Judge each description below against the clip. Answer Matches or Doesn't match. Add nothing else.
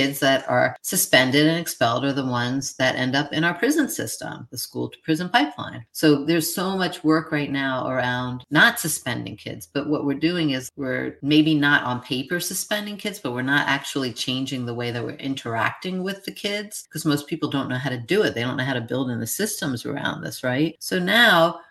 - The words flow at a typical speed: Doesn't match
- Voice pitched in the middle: Matches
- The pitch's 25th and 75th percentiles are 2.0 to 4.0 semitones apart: Doesn't match